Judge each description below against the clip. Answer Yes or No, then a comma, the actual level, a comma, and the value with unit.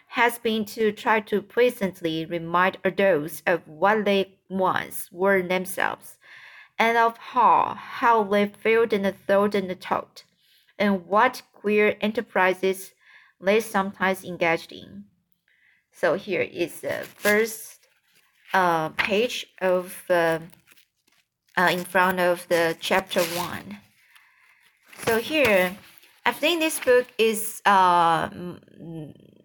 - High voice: Yes, high, 195 Hz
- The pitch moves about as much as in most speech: Yes, average, 3.7 semitones